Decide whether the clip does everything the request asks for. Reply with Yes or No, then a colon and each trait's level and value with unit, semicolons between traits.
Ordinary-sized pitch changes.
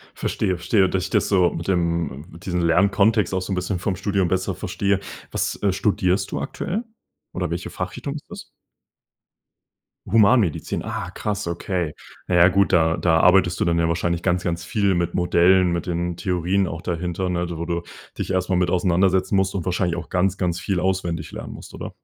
No: narrow, 2.0 semitones